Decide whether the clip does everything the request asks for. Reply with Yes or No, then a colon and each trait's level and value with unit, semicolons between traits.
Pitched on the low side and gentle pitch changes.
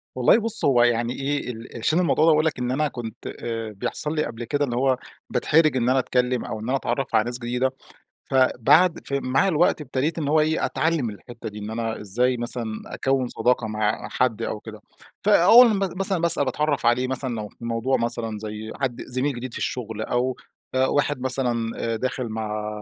No: low, 125 Hz; average, 3.8 semitones